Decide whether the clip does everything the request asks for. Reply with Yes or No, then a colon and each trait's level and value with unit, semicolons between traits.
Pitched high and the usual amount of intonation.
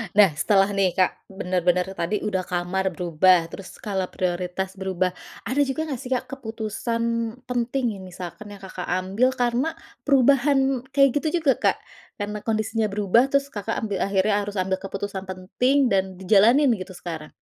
Yes: high, 205 Hz; average, 4.8 semitones